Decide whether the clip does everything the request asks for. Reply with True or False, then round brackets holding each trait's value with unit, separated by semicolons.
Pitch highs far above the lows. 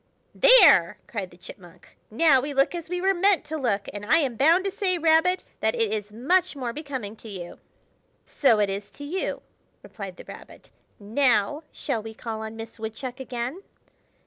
True (6.9 semitones)